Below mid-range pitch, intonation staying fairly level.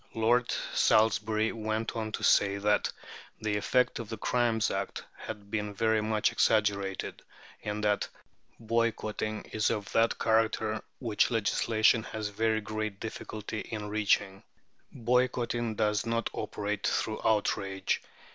Yes: low, 110 Hz; narrow, 1.4 semitones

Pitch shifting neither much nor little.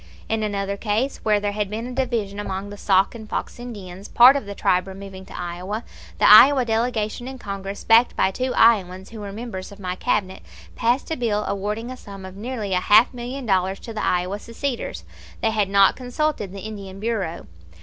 Yes: average, 3.2 semitones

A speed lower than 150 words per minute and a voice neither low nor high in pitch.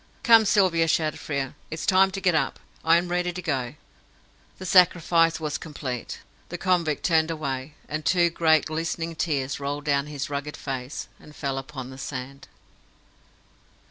No: average, 160 wpm; medium, 155 Hz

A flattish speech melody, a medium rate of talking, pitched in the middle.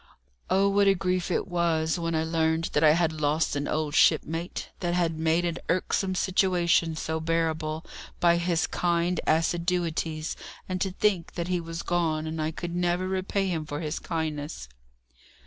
Yes: narrow, 1.9 semitones; average, 170 wpm; medium, 170 Hz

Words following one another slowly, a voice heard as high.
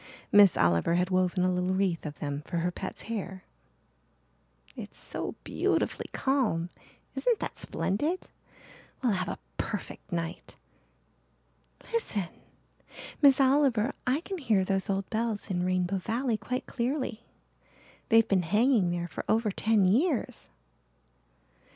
Yes: slow, 130 wpm; high, 200 Hz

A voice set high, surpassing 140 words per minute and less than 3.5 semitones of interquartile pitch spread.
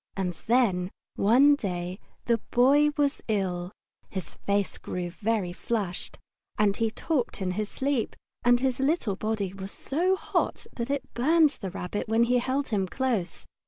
No: high, 225 Hz; average, 160 wpm; wide, 5.5 semitones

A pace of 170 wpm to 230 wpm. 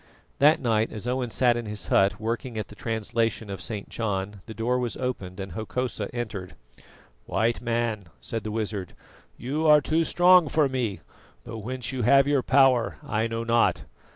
Yes: average, 180 wpm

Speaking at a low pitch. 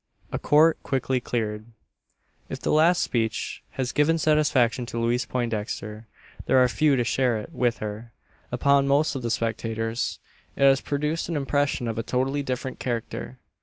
Yes: low, 125 Hz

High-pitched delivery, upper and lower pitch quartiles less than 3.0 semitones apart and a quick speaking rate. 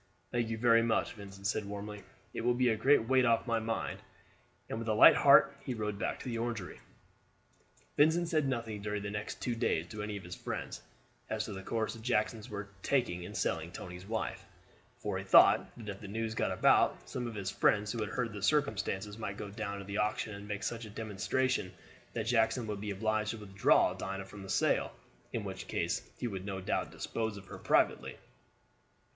No: low, 105 Hz; narrow, 2.4 semitones; fast, 210 wpm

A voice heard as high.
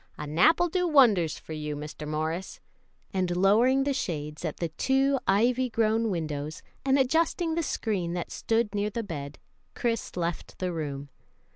Yes: high, 195 Hz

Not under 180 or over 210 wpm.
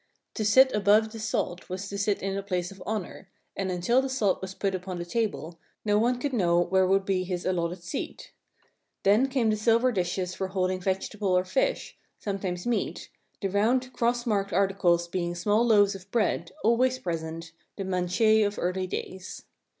Yes: average, 190 wpm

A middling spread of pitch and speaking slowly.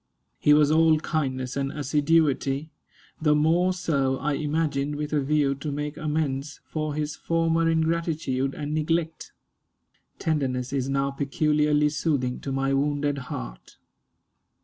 No: narrow, 2.2 semitones; slow, 130 wpm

